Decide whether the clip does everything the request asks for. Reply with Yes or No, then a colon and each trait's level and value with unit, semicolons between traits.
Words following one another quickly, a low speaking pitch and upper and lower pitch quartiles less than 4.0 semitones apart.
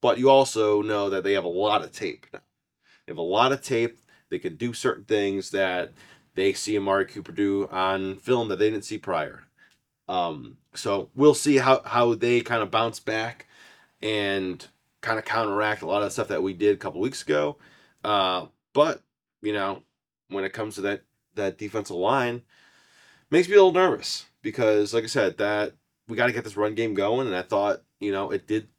Yes: fast, 210 wpm; low, 105 Hz; average, 3.1 semitones